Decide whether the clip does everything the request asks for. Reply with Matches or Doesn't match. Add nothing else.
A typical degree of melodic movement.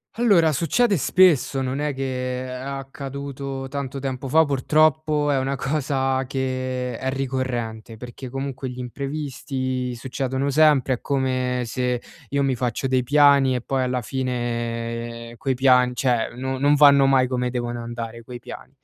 Doesn't match